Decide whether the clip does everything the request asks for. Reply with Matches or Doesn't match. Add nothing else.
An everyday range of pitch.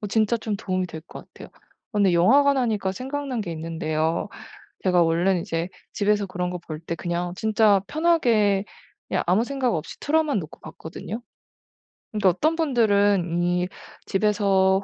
Matches